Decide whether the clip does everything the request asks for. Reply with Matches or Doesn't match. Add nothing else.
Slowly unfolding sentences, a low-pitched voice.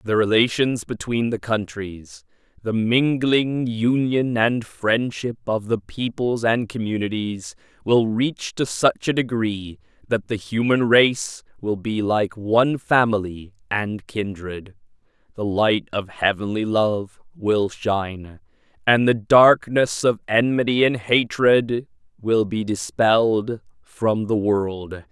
Matches